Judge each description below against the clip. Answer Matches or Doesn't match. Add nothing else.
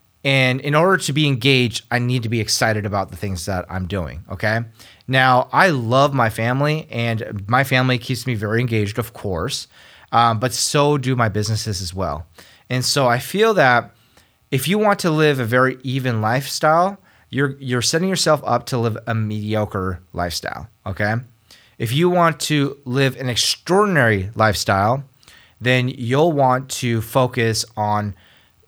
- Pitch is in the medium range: Doesn't match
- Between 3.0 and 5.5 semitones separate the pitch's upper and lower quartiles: Matches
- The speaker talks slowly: Doesn't match